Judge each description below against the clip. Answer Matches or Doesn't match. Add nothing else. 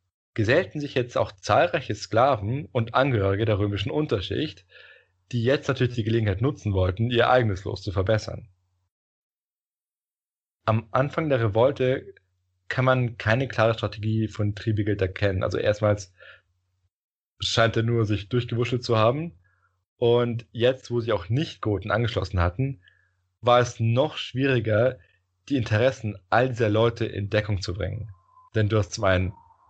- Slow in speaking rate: Doesn't match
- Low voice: Matches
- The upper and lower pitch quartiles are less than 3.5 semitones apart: Doesn't match